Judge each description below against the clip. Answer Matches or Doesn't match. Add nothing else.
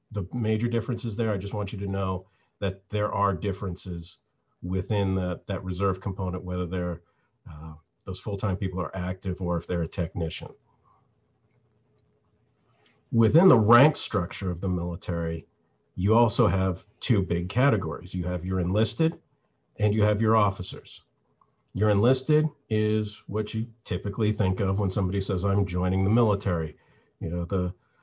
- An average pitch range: Matches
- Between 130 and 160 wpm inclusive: Matches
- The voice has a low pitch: Matches